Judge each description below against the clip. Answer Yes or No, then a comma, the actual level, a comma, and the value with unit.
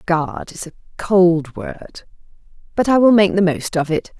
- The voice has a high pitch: No, medium, 180 Hz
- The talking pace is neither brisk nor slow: Yes, average, 185 wpm